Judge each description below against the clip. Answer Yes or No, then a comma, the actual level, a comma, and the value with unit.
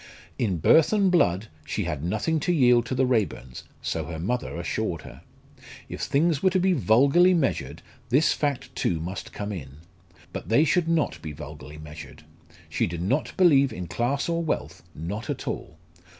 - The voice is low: Yes, low, 120 Hz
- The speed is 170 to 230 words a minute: Yes, average, 180 wpm